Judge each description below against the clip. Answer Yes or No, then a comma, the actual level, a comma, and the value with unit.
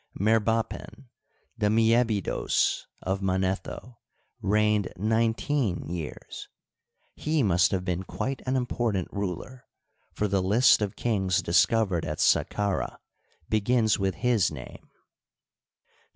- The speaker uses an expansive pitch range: No, average, 3.4 semitones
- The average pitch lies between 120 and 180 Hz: No, low, 105 Hz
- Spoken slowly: Yes, slow, 105 wpm